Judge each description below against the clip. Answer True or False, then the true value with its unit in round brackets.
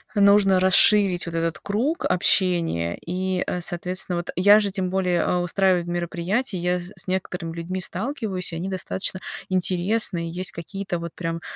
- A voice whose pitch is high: False (180 Hz)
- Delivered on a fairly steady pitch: True (1.9 semitones)